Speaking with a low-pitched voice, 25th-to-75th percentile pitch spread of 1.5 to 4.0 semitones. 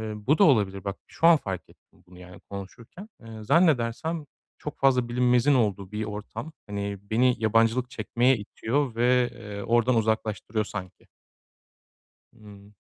Yes: low, 115 Hz; average, 3.6 semitones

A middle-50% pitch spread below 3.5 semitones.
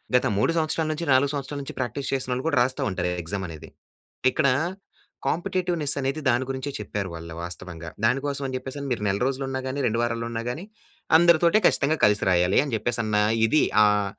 No: wide, 5.5 semitones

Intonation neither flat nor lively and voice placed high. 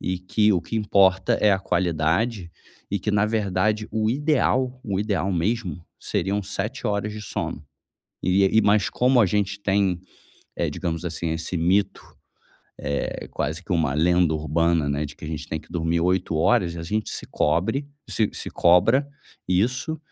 No: average, 4.1 semitones; very low, 95 Hz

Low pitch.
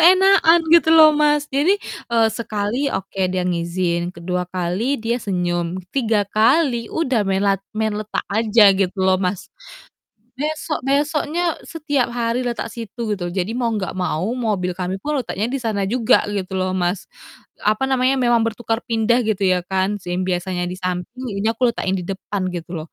No: high, 215 Hz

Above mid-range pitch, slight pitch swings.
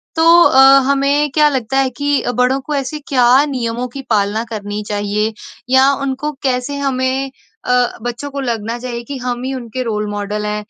No: very high, 255 Hz; average, 3.2 semitones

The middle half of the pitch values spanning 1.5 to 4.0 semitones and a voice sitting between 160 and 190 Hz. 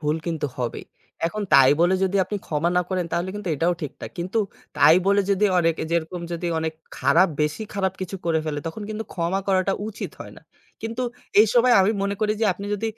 Yes: average, 3.6 semitones; medium, 185 Hz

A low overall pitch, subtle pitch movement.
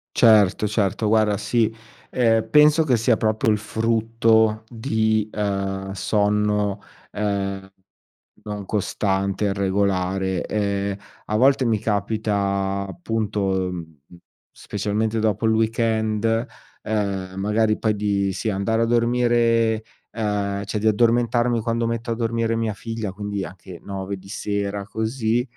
Yes: low, 105 Hz; narrow, 2.3 semitones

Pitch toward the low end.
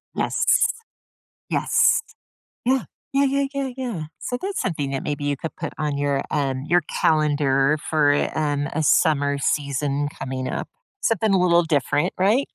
No: medium, 150 Hz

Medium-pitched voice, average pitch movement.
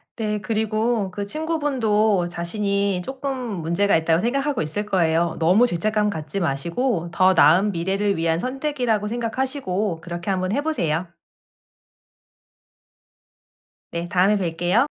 No: high, 200 Hz; average, 4.9 semitones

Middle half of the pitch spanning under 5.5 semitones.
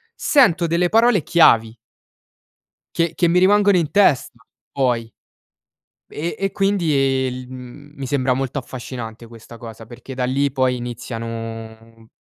No: wide, 6.4 semitones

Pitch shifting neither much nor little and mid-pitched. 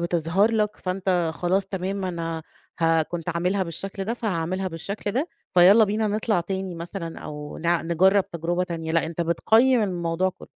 Yes: average, 3.0 semitones; medium, 180 Hz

